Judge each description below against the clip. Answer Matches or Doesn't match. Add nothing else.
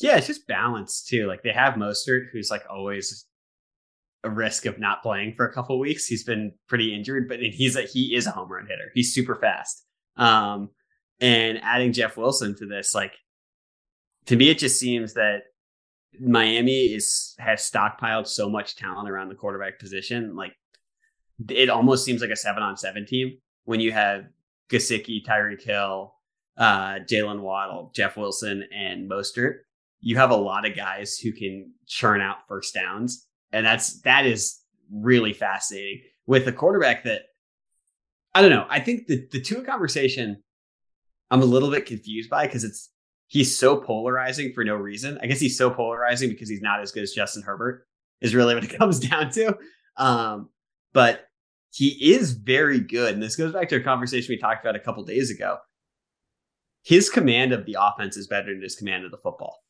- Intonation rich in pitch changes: Doesn't match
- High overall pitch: Doesn't match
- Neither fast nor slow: Matches